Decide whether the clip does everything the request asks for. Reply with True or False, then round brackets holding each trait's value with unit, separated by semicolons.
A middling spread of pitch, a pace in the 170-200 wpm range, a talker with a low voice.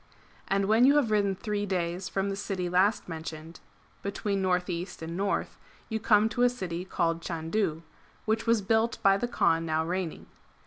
False (3.9 semitones; 180 wpm; 195 Hz)